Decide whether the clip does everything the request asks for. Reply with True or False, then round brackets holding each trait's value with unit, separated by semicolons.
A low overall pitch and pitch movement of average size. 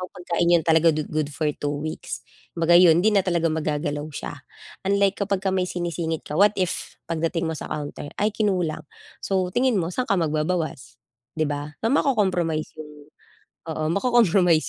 False (170 Hz; 3.5 semitones)